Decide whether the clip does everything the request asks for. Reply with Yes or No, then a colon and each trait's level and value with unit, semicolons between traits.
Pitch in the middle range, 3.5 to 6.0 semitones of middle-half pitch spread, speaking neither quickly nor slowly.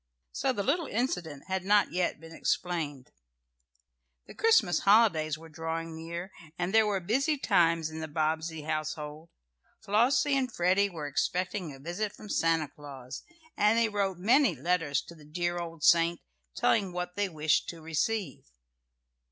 Yes: medium, 175 Hz; average, 4.4 semitones; average, 155 wpm